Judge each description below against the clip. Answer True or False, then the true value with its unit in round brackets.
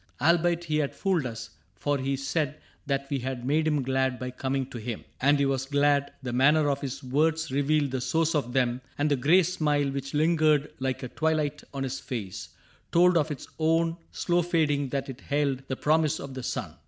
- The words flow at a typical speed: False (210 wpm)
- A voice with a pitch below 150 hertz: True (140 Hz)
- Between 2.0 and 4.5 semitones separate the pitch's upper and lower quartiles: True (2.9 semitones)